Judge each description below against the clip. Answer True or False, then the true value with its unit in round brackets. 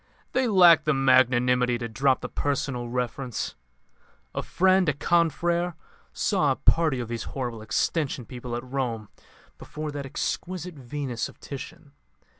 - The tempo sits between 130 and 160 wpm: True (140 wpm)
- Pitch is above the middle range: False (135 Hz)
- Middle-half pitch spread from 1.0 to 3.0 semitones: False (4.8 semitones)